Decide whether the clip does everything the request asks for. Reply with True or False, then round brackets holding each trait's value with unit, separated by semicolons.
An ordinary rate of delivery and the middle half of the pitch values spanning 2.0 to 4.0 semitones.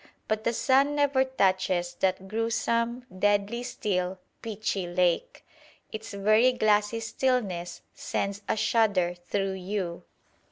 False (115 wpm; 3.7 semitones)